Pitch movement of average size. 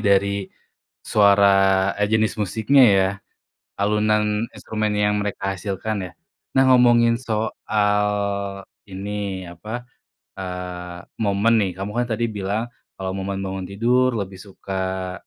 No: narrow, 2.2 semitones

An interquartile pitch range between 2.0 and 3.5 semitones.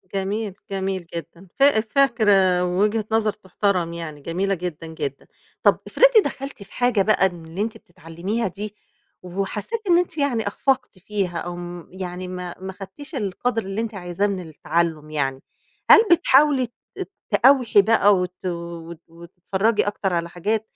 No: average, 4.1 semitones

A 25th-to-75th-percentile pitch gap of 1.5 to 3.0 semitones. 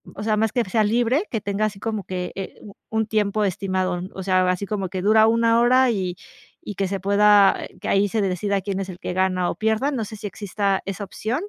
Yes: narrow, 2.6 semitones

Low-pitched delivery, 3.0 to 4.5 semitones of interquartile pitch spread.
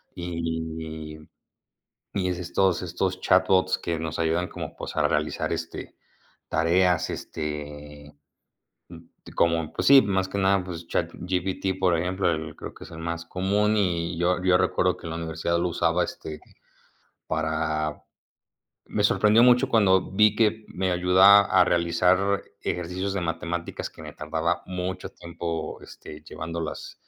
No: very low, 90 Hz; narrow, 2.4 semitones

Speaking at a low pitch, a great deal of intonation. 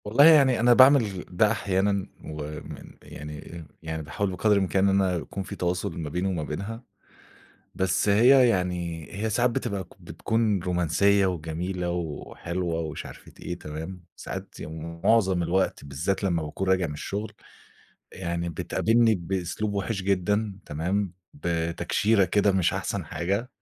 No: very low, 95 Hz; average, 3.3 semitones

